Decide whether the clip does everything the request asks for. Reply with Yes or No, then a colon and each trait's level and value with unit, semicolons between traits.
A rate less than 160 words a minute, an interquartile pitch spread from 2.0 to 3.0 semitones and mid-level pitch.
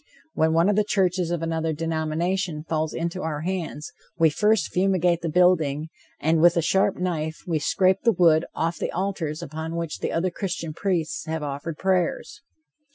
No: average, 170 wpm; narrow, 2.5 semitones; medium, 165 Hz